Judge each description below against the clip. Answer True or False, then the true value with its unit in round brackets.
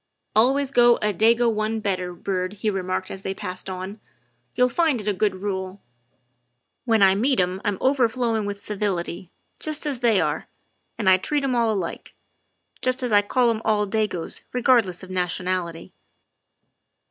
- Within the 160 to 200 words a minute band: True (175 wpm)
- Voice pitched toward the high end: True (205 Hz)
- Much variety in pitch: False (4.1 semitones)